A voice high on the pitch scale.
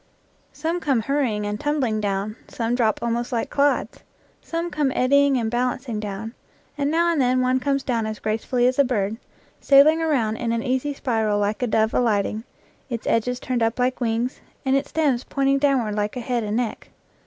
Yes: high, 245 Hz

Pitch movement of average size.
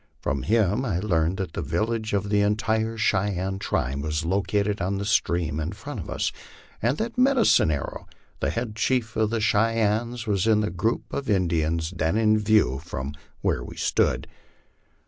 Yes: average, 4.4 semitones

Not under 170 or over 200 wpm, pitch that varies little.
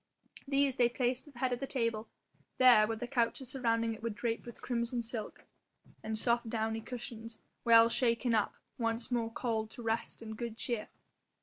Yes: average, 185 wpm; narrow, 1.5 semitones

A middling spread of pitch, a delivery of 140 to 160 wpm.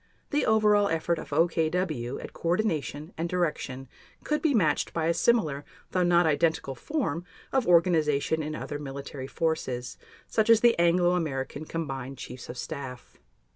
Yes: average, 4.3 semitones; average, 155 wpm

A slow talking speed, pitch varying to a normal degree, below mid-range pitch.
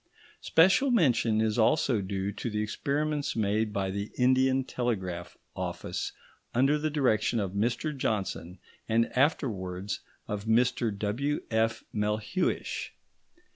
Yes: slow, 115 wpm; average, 4.6 semitones; low, 115 Hz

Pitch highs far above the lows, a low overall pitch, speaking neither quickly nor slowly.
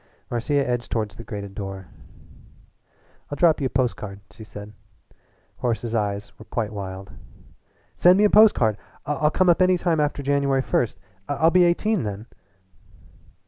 Yes: wide, 7.1 semitones; low, 125 Hz; average, 160 wpm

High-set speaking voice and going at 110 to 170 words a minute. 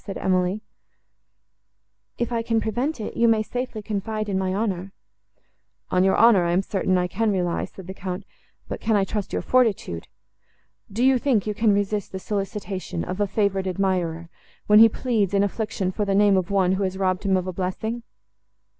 No: high, 200 Hz; average, 190 wpm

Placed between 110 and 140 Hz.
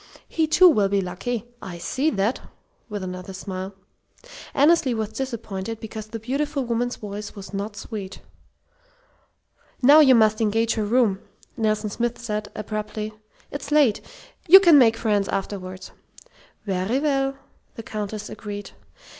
No: high, 215 Hz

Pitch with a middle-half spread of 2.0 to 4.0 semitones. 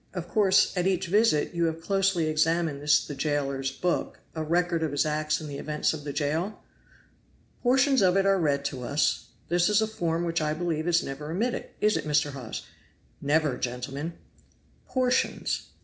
Yes: average, 3.6 semitones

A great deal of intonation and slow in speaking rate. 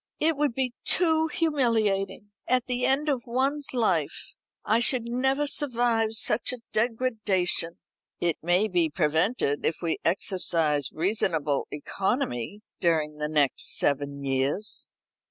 Yes: wide, 7.7 semitones; slow, 125 wpm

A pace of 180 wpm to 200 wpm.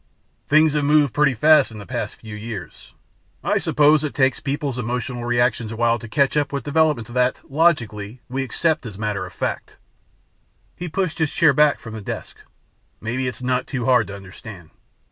Yes: average, 185 wpm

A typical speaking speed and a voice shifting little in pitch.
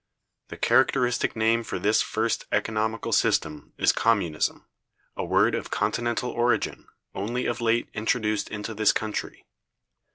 No: slow, 130 wpm; narrow, 1.8 semitones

